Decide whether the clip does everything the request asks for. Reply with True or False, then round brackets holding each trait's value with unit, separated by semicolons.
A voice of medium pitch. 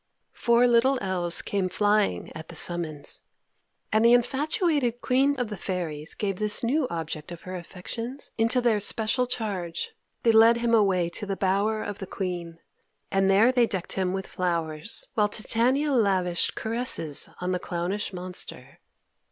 False (205 Hz)